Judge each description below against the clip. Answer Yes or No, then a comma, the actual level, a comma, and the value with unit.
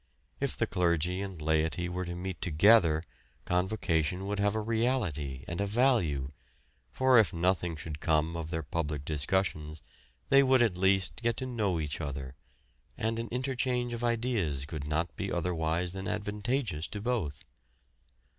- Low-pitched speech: Yes, very low, 90 Hz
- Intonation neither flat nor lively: No, wide, 5.8 semitones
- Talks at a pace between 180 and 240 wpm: No, average, 155 wpm